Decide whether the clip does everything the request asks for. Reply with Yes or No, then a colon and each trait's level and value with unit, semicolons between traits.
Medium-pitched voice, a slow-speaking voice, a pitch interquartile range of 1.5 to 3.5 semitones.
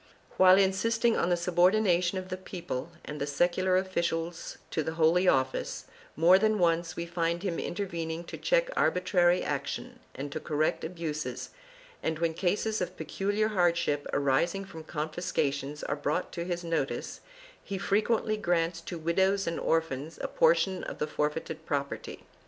No: medium, 170 Hz; average, 155 wpm; average, 2.8 semitones